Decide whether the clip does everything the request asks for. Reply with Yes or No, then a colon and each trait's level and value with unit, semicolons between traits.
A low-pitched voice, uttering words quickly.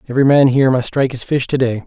Yes: low, 130 Hz; fast, 290 wpm